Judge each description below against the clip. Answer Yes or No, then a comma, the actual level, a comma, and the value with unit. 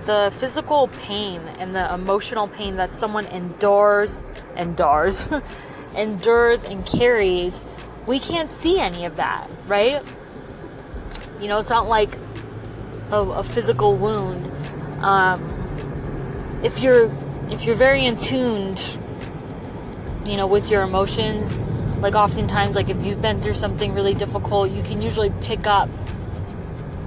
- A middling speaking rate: No, slow, 130 wpm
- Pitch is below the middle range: No, high, 195 Hz